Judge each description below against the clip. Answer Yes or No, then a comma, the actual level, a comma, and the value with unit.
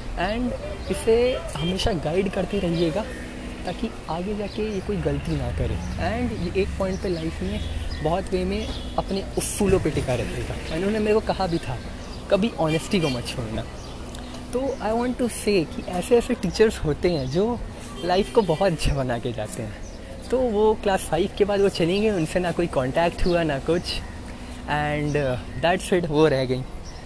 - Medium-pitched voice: Yes, medium, 170 Hz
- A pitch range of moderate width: No, wide, 7.8 semitones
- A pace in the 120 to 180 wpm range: Yes, average, 175 wpm